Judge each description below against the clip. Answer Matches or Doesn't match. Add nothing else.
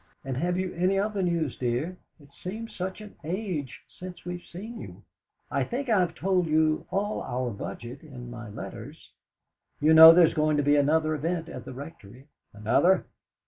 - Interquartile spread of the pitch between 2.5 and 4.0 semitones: Doesn't match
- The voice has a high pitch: Doesn't match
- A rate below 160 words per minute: Doesn't match